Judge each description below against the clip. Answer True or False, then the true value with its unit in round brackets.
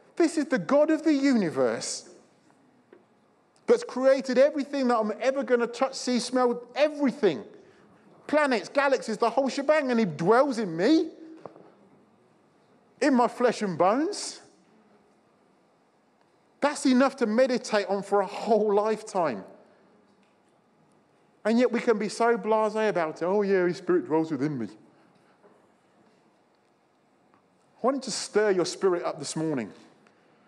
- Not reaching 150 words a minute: True (135 wpm)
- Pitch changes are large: False (4.8 semitones)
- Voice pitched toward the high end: True (240 Hz)